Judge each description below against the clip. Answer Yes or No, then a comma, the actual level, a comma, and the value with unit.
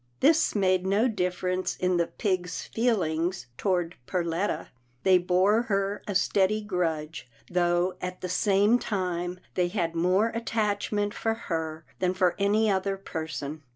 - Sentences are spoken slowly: No, average, 145 wpm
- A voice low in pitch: No, medium, 185 Hz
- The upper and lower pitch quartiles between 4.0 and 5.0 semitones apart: No, average, 2.8 semitones